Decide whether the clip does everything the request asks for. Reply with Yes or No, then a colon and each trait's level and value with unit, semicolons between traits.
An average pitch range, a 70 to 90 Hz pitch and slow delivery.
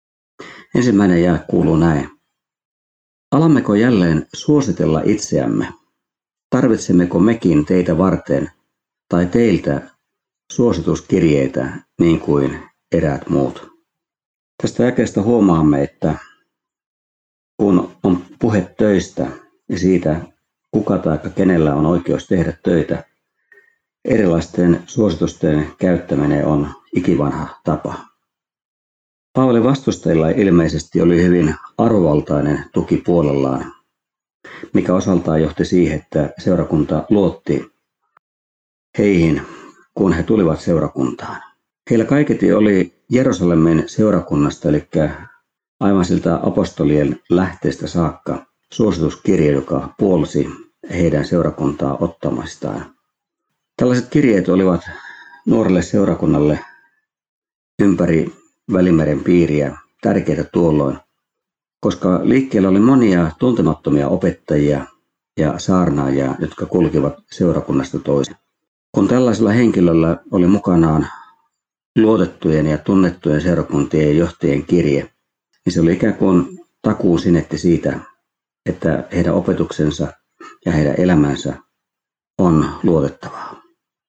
Yes: average, 4.3 semitones; very low, 85 Hz; slow, 90 wpm